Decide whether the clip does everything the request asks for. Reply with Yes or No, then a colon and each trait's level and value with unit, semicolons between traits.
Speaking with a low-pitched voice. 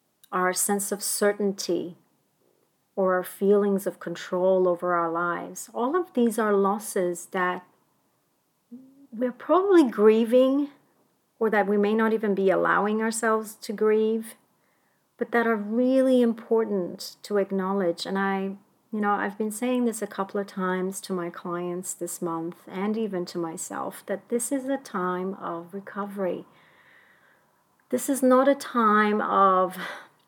No: high, 205 Hz